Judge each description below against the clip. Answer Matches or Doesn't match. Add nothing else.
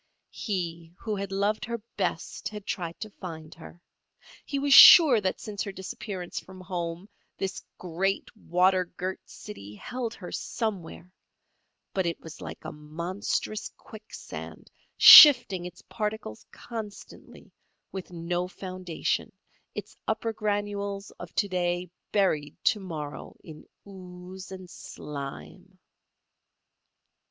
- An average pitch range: Matches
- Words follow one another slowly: Matches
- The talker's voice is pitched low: Doesn't match